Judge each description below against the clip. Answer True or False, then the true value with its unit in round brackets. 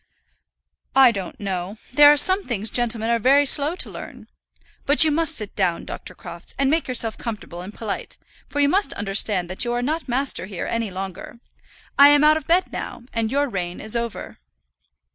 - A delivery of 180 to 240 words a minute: True (195 wpm)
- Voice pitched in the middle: False (235 Hz)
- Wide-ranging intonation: True (5.9 semitones)